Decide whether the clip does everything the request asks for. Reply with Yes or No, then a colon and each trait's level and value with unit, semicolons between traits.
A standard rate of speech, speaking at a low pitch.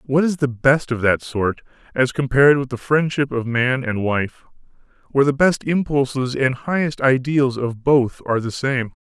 Yes: average, 185 wpm; low, 130 Hz